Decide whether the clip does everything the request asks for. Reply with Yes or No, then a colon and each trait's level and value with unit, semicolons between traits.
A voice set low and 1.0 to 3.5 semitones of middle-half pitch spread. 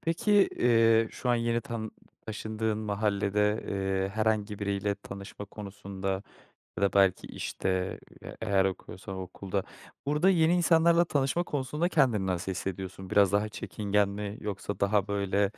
Yes: low, 105 Hz; average, 2.9 semitones